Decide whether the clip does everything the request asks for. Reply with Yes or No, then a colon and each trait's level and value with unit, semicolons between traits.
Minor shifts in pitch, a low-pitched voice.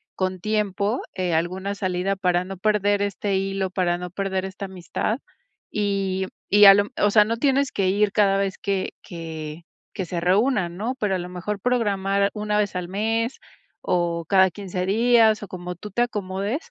No: narrow, 2.3 semitones; high, 195 Hz